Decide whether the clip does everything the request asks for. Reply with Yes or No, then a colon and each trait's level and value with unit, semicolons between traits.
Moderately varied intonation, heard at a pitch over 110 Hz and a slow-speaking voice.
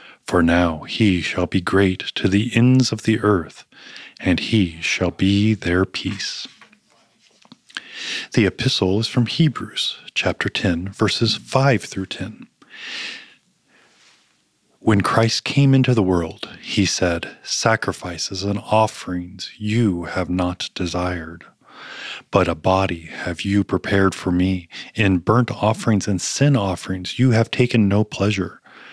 No: average, 3.7 semitones; low, 100 Hz; slow, 130 wpm